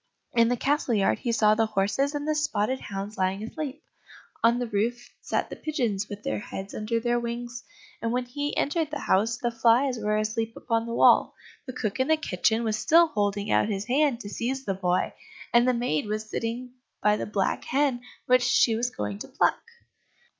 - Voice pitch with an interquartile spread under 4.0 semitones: Yes, average, 3.2 semitones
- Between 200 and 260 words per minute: Yes, fast, 205 wpm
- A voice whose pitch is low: No, high, 230 Hz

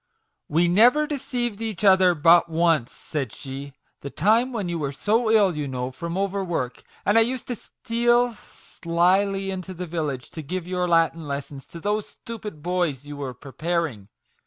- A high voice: No, medium, 175 Hz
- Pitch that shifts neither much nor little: No, wide, 5.7 semitones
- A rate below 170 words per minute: No, average, 185 wpm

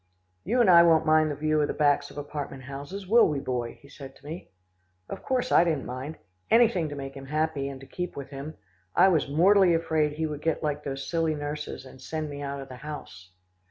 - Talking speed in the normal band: No, fast, 230 wpm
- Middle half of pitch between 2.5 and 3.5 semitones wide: Yes, average, 2.8 semitones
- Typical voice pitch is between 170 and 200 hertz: No, medium, 150 Hz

